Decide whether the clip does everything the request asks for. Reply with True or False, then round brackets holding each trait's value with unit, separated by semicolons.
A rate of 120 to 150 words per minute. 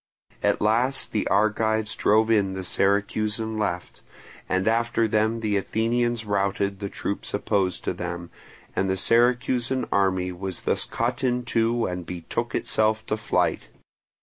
True (145 wpm)